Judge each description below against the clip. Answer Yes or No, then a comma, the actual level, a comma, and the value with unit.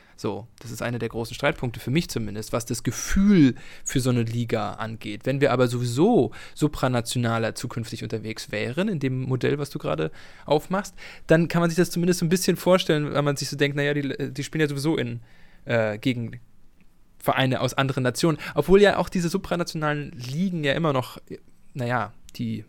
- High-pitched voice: No, low, 135 Hz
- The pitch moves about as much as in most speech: Yes, average, 5.0 semitones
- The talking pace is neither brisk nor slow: Yes, average, 190 wpm